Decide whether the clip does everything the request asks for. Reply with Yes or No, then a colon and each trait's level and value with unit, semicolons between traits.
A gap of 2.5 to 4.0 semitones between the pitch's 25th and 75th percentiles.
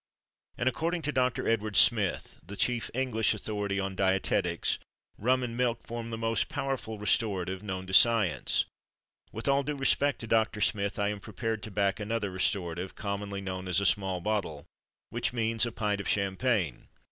Yes: average, 3.1 semitones